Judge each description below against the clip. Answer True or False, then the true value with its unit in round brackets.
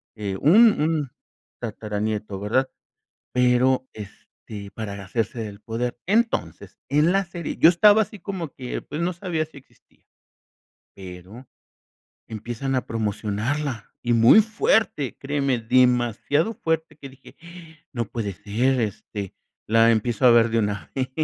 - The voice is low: True (125 Hz)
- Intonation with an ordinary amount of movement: False (5.8 semitones)